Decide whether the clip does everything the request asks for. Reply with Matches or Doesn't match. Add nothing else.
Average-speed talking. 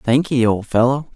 Matches